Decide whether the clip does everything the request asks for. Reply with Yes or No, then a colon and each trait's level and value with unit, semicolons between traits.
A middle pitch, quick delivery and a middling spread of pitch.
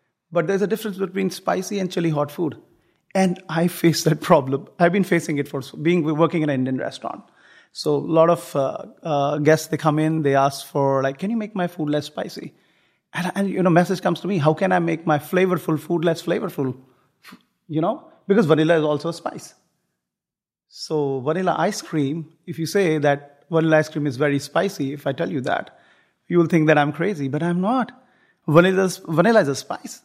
Yes: medium, 165 Hz; fast, 210 wpm; average, 3.6 semitones